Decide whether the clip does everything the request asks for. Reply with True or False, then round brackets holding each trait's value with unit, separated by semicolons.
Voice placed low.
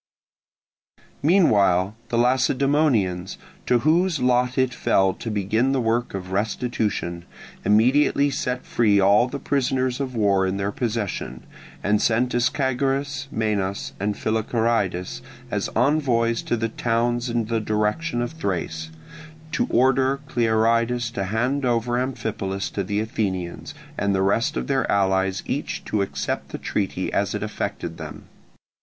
True (115 Hz)